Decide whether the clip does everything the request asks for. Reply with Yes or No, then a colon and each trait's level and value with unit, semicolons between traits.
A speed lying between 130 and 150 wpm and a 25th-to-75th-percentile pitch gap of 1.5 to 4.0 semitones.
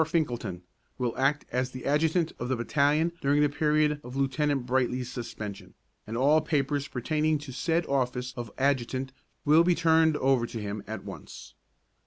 No: average, 160 wpm; average, 3.4 semitones